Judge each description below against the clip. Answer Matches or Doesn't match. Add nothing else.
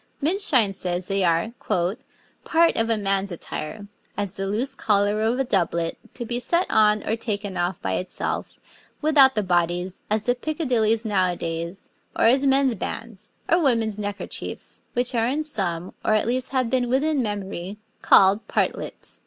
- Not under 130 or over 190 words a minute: Matches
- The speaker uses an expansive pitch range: Doesn't match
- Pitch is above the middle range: Matches